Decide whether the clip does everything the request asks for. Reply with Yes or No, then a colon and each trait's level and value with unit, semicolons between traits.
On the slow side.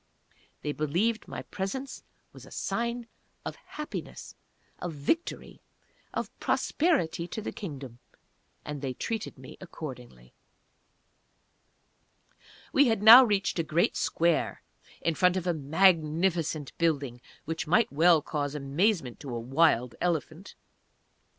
Yes: slow, 120 wpm